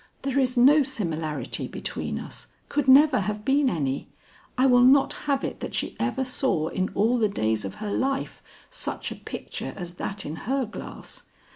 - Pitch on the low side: No, high, 245 Hz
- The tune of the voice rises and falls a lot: Yes, wide, 6.4 semitones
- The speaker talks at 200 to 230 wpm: No, average, 180 wpm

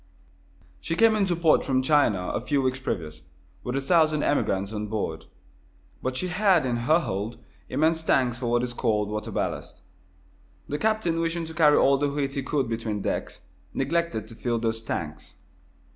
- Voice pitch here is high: No, low, 135 Hz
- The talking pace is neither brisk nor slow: Yes, average, 175 wpm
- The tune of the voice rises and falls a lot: Yes, wide, 6.2 semitones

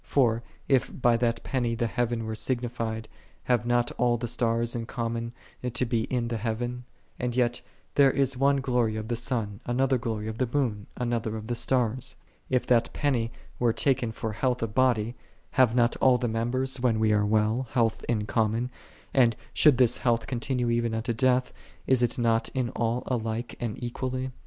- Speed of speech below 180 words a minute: No, average, 190 wpm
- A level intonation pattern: Yes, narrow, 1.8 semitones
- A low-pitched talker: Yes, low, 120 Hz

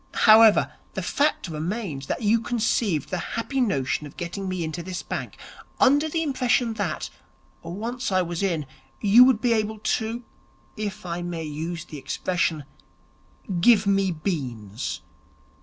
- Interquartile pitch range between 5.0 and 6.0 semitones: Yes, wide, 5.6 semitones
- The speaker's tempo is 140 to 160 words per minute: Yes, average, 145 wpm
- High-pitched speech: Yes, high, 195 Hz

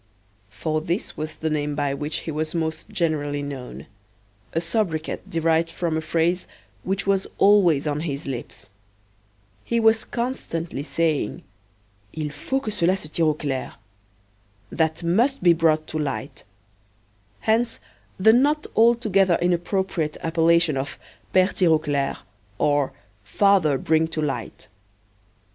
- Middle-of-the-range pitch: Yes, medium, 165 Hz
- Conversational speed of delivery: No, slow, 130 wpm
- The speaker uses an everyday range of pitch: Yes, average, 4.0 semitones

